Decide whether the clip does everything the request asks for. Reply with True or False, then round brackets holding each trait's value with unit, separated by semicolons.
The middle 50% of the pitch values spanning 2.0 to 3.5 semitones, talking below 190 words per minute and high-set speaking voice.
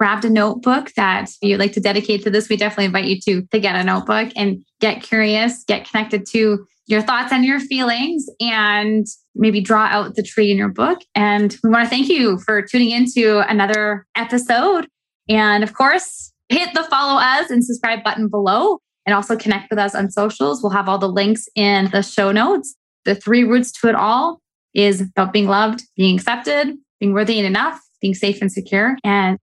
False (3.1 semitones; 200 wpm; 215 Hz)